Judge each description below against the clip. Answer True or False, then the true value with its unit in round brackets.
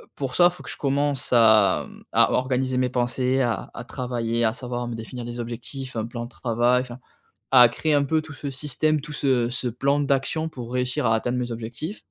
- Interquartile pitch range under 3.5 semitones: True (2.6 semitones)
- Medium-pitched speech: False (125 Hz)